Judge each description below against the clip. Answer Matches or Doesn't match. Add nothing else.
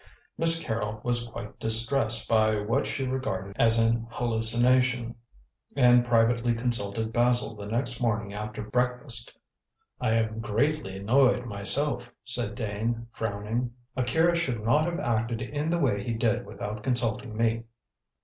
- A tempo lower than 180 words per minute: Matches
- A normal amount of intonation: Doesn't match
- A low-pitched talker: Matches